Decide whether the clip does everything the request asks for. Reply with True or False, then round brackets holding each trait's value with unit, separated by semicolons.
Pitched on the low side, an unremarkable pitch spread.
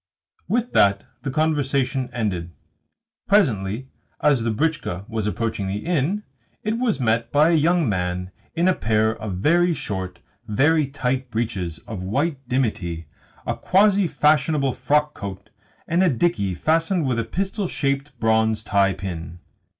False (130 Hz; 7.4 semitones)